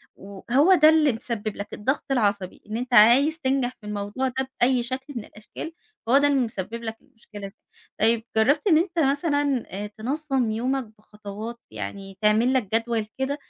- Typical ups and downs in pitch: Yes, average, 4.4 semitones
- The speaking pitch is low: No, high, 240 Hz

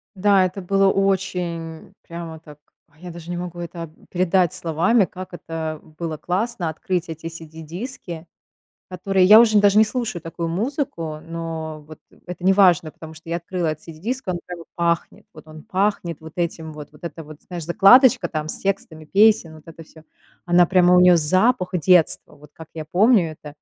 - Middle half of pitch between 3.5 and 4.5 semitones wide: No, average, 2.9 semitones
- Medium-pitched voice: Yes, medium, 170 Hz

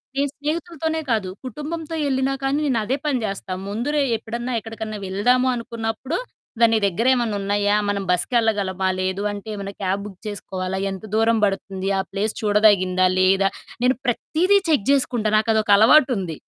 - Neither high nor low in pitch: No, high, 220 Hz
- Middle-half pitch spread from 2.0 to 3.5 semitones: No, average, 4.6 semitones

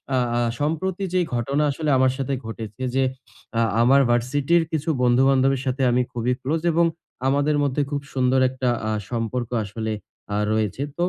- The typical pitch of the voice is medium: No, low, 130 Hz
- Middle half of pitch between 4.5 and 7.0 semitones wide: No, average, 3.1 semitones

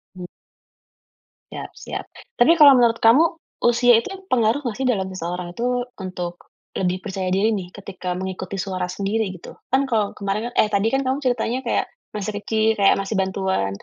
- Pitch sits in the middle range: No, high, 205 Hz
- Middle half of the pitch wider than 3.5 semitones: Yes, average, 4.3 semitones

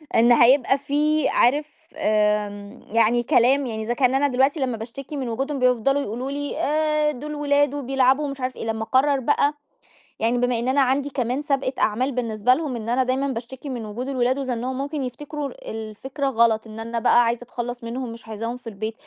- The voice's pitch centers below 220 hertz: No, very high, 255 Hz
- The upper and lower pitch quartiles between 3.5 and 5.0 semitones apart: No, average, 3.1 semitones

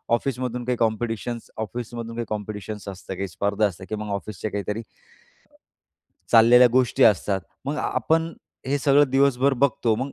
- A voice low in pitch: Yes, low, 115 Hz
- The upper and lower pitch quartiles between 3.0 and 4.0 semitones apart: Yes, average, 3.5 semitones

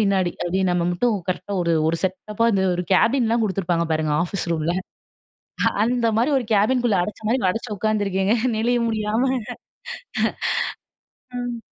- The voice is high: Yes, high, 205 Hz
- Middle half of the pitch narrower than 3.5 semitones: No, average, 4.3 semitones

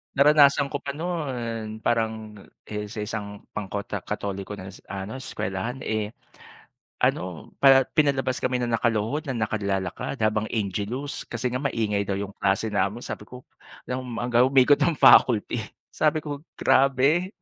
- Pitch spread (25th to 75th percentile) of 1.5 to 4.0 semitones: No, average, 4.5 semitones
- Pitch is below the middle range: Yes, low, 115 Hz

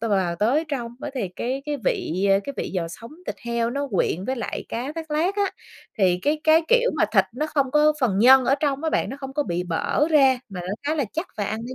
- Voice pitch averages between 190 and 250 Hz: No, very high, 265 Hz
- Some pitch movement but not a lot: No, wide, 6.4 semitones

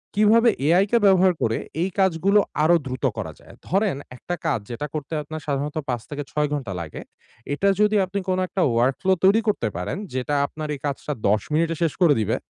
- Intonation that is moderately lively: No, wide, 5.8 semitones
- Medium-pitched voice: Yes, medium, 155 Hz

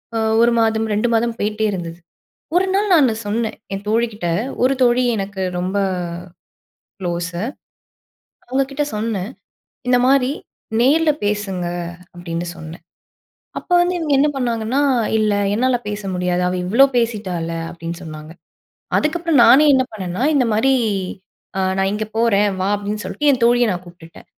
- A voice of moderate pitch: No, high, 215 Hz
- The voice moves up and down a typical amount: No, wide, 5.7 semitones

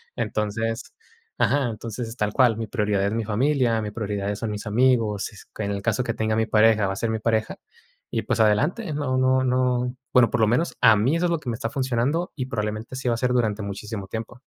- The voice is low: Yes, low, 115 Hz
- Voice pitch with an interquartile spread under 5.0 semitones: Yes, average, 3.1 semitones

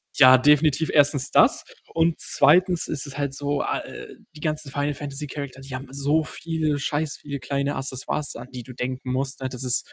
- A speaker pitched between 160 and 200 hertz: No, medium, 140 Hz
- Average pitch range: No, narrow, 2.1 semitones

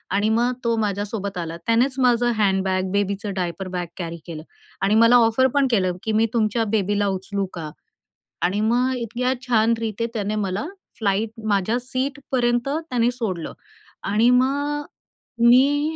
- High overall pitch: Yes, high, 220 Hz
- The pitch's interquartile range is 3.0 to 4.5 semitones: Yes, average, 3.7 semitones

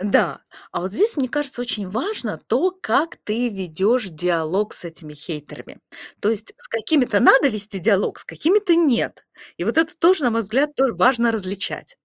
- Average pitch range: No, wide, 7.0 semitones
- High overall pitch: Yes, high, 230 Hz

